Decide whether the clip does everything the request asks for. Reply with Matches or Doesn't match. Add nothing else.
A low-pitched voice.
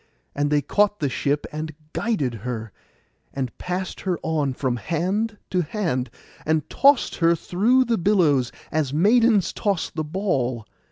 Doesn't match